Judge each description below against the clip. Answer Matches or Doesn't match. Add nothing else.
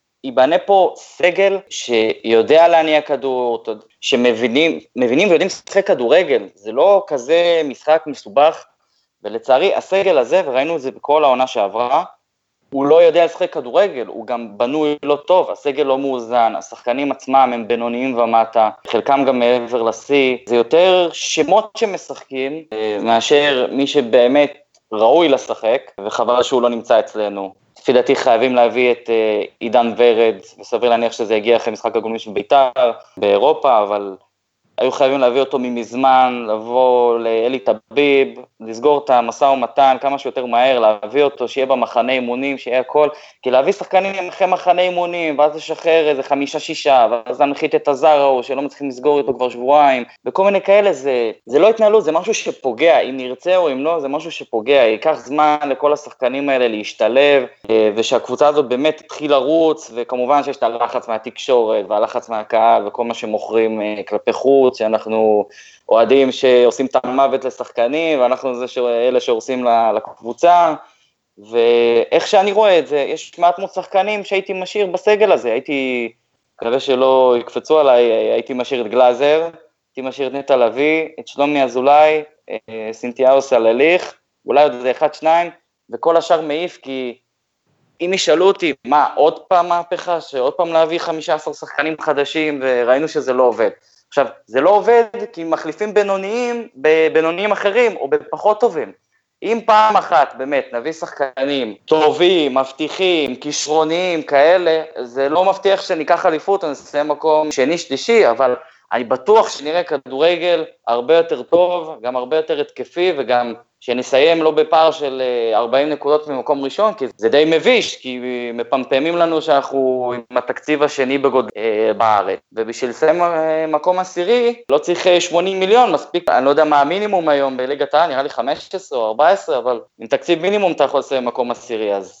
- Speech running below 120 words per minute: Doesn't match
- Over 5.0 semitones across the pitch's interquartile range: Matches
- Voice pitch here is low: Doesn't match